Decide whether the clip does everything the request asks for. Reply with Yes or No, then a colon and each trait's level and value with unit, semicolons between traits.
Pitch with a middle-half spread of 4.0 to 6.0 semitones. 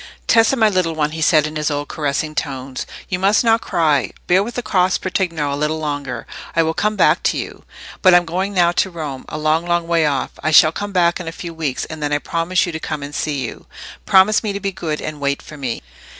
No: average, 3.5 semitones